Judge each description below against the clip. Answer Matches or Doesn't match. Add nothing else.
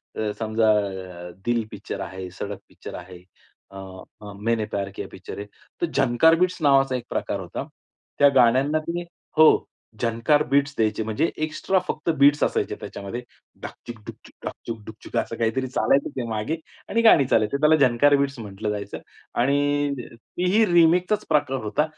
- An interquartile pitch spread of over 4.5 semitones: Matches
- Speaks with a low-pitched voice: Matches